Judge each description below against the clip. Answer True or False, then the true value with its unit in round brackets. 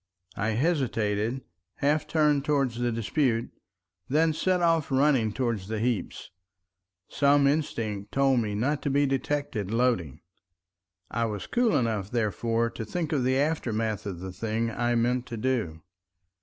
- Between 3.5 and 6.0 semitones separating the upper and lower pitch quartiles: True (4.5 semitones)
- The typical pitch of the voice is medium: False (120 Hz)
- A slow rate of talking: False (145 wpm)